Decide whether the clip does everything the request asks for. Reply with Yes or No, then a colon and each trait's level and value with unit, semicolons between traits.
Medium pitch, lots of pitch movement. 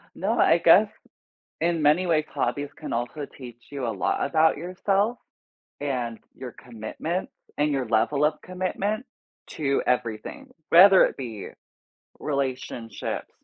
Yes: medium, 145 Hz; wide, 5.9 semitones